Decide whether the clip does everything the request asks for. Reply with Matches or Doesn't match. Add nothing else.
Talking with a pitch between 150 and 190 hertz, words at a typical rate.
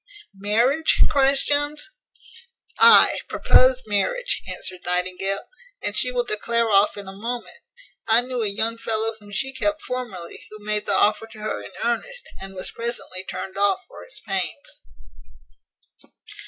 Doesn't match